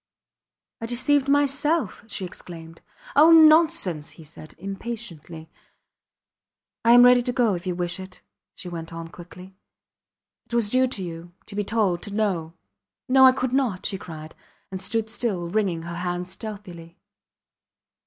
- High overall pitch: Yes, high, 195 Hz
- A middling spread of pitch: No, wide, 6.0 semitones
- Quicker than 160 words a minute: No, average, 155 wpm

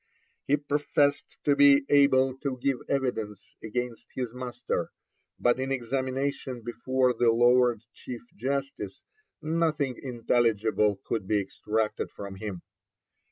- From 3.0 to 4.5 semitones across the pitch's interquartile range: Yes, average, 3.4 semitones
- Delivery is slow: Yes, slow, 115 wpm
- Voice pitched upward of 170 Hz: No, low, 125 Hz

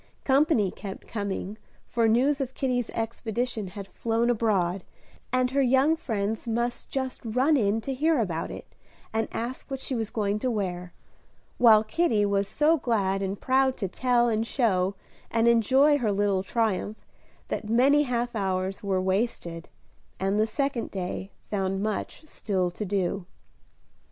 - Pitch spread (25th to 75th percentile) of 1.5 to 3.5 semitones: No, average, 4.2 semitones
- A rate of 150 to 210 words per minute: Yes, average, 155 wpm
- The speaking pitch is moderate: No, high, 225 Hz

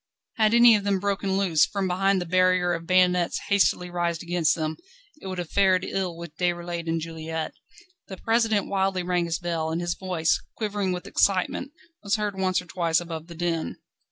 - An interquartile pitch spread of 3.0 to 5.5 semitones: No, narrow, 2.4 semitones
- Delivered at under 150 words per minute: No, average, 190 wpm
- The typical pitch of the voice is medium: Yes, medium, 180 Hz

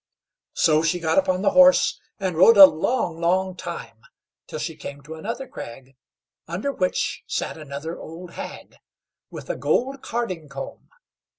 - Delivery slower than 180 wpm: Yes, average, 155 wpm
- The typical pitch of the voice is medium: Yes, medium, 175 Hz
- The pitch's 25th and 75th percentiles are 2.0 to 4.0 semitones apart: No, average, 5.0 semitones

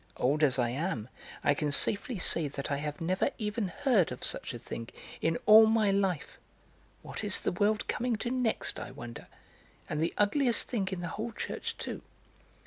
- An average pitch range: No, wide, 7.0 semitones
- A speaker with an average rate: Yes, average, 190 wpm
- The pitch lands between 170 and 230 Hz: Yes, medium, 185 Hz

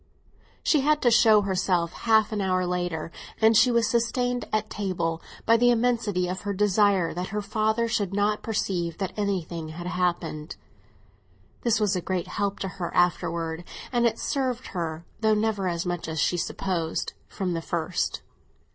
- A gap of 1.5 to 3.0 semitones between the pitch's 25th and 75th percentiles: No, average, 3.9 semitones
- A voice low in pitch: No, high, 195 Hz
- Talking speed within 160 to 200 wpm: Yes, average, 170 wpm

